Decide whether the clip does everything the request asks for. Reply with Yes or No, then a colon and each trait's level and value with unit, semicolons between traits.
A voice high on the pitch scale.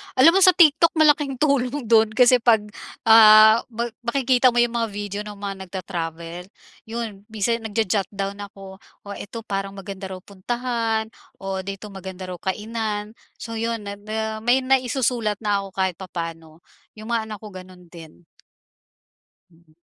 Yes: high, 215 Hz